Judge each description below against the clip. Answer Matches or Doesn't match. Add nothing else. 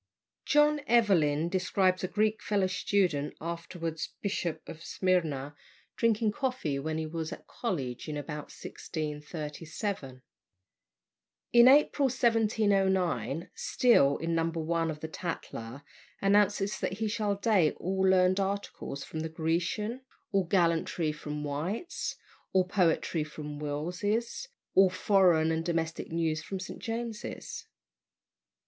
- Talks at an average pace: Doesn't match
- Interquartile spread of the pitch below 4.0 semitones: Doesn't match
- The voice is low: Doesn't match